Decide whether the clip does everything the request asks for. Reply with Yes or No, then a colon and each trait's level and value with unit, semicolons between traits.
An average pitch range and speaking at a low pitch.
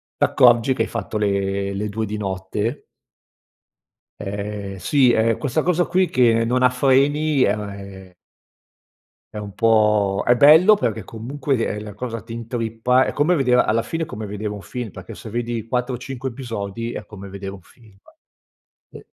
Yes: average, 3.7 semitones; low, 115 Hz